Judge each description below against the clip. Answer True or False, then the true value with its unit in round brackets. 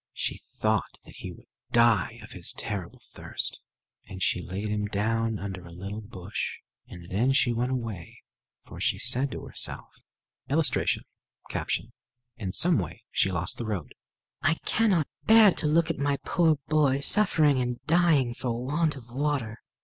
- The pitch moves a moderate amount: False (6.4 semitones)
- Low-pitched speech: True (120 Hz)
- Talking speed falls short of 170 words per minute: True (160 wpm)